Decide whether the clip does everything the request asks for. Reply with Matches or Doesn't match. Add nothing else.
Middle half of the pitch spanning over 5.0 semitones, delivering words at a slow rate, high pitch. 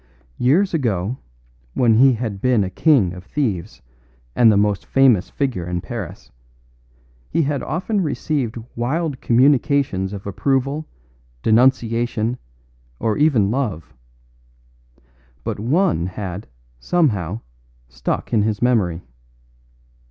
Doesn't match